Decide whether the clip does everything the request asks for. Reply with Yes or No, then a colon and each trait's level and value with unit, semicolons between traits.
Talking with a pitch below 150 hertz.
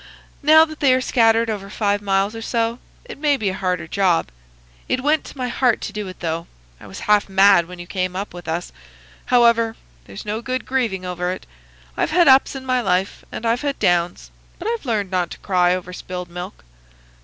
No: high, 205 Hz